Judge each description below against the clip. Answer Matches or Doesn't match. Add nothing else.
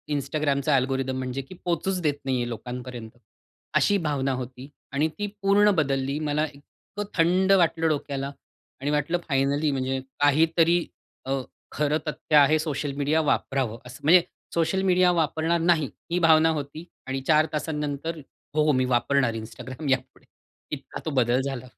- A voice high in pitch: Doesn't match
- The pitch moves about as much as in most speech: Matches